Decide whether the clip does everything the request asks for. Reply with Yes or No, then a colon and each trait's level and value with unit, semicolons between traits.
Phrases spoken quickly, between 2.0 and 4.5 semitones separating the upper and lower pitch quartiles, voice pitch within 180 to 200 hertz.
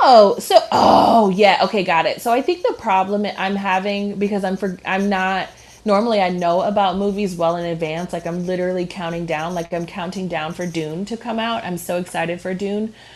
Yes: fast, 210 wpm; average, 2.8 semitones; high, 190 Hz